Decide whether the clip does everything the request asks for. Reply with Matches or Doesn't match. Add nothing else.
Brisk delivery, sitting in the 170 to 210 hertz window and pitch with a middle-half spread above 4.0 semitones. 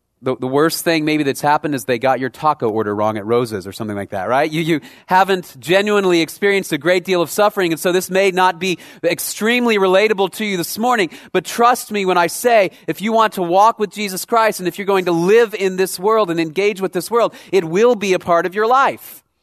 Matches